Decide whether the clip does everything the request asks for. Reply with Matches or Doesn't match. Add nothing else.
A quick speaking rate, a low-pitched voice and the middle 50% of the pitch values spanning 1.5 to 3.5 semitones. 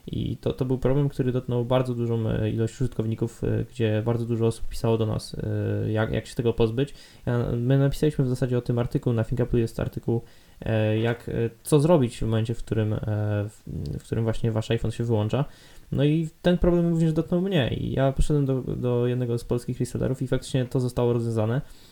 Matches